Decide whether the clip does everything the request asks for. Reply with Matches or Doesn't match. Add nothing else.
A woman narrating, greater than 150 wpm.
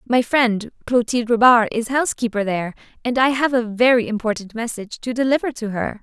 Matches